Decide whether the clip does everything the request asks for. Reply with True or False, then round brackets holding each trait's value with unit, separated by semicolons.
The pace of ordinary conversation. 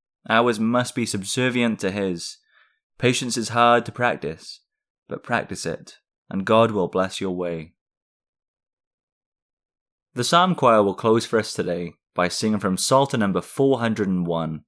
True (150 wpm)